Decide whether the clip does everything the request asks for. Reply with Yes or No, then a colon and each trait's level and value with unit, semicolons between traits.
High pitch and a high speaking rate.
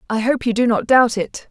Yes: high, 235 Hz; fast, 280 wpm